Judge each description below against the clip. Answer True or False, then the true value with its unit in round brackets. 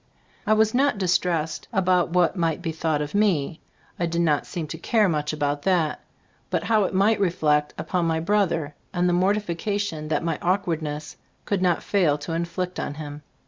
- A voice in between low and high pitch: True (170 Hz)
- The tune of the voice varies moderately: True (3.6 semitones)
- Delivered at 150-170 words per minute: False (185 wpm)